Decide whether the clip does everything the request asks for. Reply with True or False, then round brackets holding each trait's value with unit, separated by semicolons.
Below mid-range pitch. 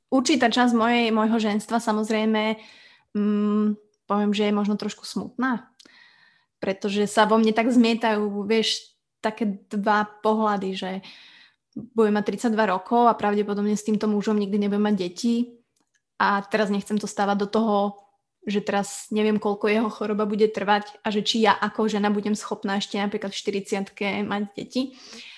False (210 Hz)